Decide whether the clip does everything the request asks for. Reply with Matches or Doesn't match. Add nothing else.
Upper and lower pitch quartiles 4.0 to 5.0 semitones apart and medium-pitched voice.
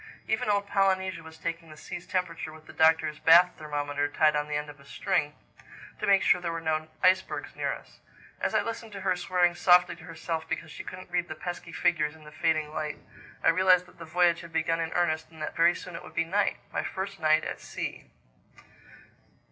Doesn't match